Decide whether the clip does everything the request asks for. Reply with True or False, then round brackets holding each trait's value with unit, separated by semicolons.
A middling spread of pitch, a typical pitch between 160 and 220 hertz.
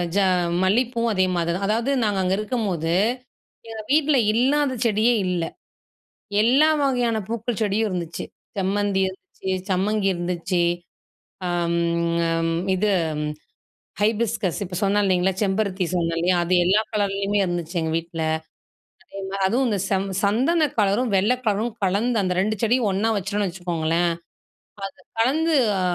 True (3.8 semitones; 200 Hz)